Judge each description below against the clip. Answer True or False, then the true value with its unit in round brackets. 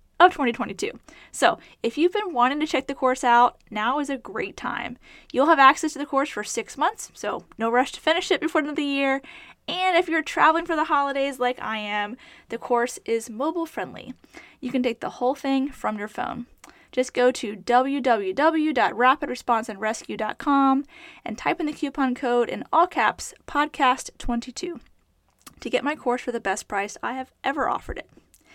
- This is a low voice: False (270 Hz)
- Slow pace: False (185 wpm)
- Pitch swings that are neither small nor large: True (4.4 semitones)